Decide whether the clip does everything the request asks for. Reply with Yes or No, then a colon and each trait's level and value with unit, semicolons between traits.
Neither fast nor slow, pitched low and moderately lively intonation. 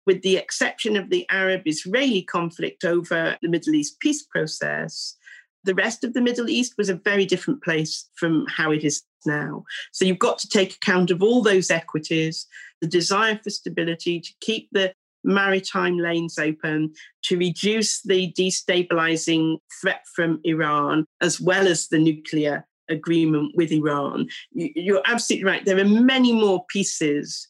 No: average, 160 wpm; medium, 185 Hz; average, 3.8 semitones